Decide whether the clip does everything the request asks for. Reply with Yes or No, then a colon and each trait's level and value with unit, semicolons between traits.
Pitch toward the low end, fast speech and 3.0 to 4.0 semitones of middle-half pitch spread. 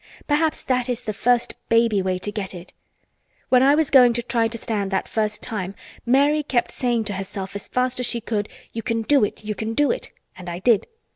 No: high, 230 Hz; fast, 225 wpm; average, 3.5 semitones